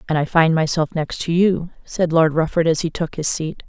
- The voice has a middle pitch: Yes, medium, 160 Hz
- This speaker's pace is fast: Yes, fast, 245 wpm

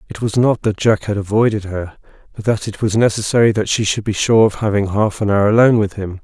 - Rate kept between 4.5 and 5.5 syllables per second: No, 6.0 syllables/s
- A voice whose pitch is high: No, low, 105 Hz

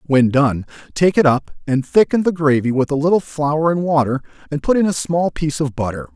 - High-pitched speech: No, medium, 150 Hz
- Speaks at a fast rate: Yes, fast, 225 wpm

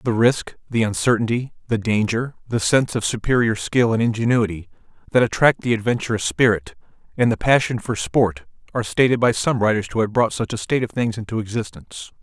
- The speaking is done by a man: Yes, male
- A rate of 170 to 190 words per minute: Yes, average, 185 wpm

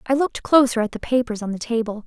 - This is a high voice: Yes, high, 235 Hz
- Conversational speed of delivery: No, fast, 260 wpm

